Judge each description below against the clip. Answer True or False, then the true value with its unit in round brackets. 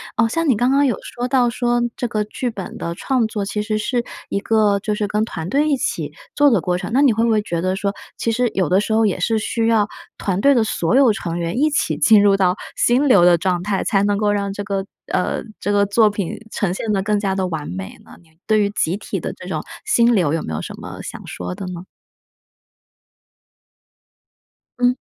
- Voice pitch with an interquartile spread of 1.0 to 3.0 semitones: False (3.6 semitones)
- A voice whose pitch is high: True (210 Hz)